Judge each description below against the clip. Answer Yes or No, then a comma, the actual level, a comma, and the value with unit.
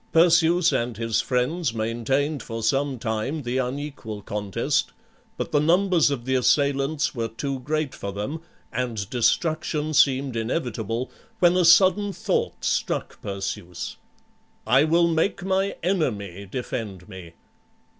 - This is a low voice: Yes, low, 130 Hz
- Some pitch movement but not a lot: No, wide, 5.8 semitones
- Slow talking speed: Yes, slow, 130 wpm